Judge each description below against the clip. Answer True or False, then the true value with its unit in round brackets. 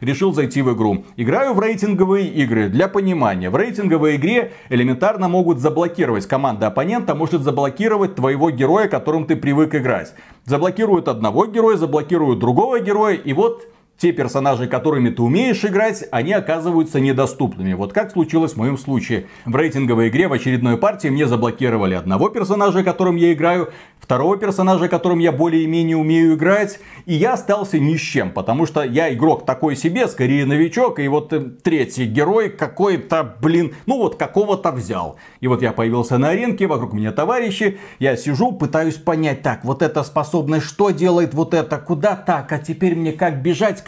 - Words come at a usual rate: False (165 wpm)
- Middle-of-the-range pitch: True (160 Hz)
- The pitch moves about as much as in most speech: False (5.7 semitones)